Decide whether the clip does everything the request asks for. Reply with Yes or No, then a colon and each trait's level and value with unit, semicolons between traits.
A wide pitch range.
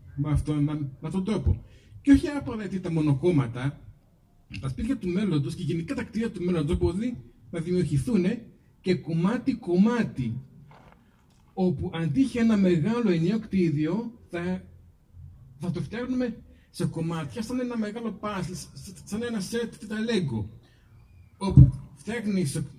Yes: wide, 7.4 semitones